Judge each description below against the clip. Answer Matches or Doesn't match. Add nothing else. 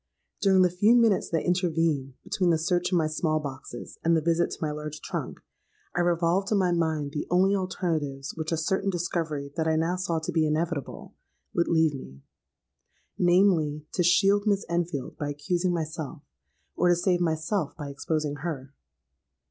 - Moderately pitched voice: Matches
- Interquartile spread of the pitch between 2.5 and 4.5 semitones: Matches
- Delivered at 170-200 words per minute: Matches